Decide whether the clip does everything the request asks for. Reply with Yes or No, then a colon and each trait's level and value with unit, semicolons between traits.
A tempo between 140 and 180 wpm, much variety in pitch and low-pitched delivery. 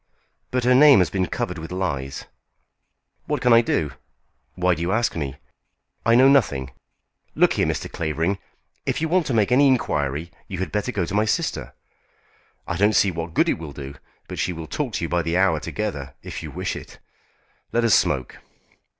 No: average, 200 wpm; wide, 6.4 semitones; very low, 90 Hz